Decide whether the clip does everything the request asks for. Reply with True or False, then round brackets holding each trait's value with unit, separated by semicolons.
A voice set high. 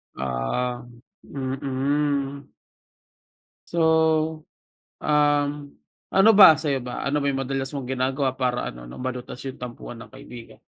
False (135 Hz)